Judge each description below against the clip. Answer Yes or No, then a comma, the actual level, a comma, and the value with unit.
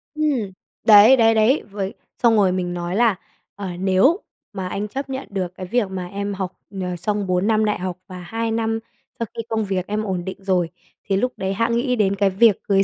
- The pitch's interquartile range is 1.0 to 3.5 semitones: Yes, average, 3.2 semitones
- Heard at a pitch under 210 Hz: Yes, high, 200 Hz